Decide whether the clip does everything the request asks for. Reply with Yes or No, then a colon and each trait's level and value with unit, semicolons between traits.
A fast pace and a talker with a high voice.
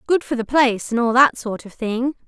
Yes: fast, 240 wpm; high, 245 Hz